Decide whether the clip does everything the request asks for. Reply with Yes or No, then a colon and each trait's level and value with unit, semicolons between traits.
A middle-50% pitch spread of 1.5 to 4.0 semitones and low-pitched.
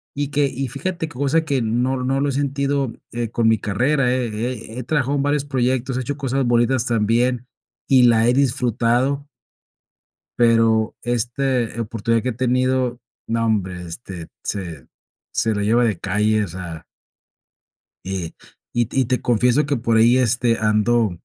Yes: average, 3.0 semitones; low, 120 Hz